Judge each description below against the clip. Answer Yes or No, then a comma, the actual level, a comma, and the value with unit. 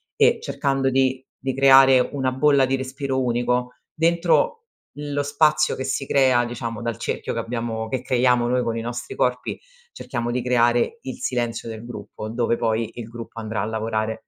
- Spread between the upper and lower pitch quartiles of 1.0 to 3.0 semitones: Yes, narrow, 2.4 semitones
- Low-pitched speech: Yes, low, 125 Hz